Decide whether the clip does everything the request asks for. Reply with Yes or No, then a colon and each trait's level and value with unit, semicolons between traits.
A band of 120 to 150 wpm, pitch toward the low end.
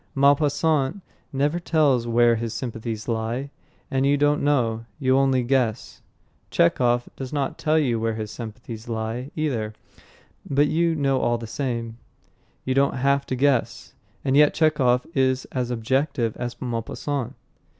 Yes: average, 145 wpm; low, 130 Hz